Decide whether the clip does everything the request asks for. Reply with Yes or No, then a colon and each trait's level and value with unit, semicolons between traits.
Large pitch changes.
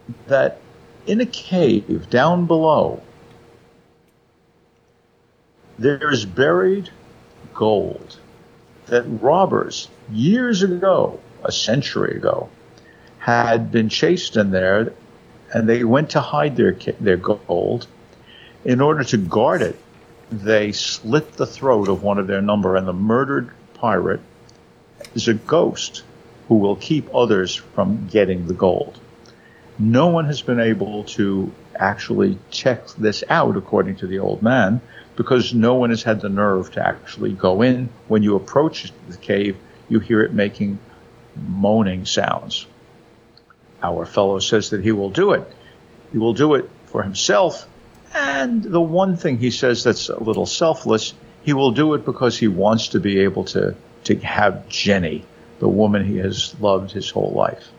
No: average, 4.3 semitones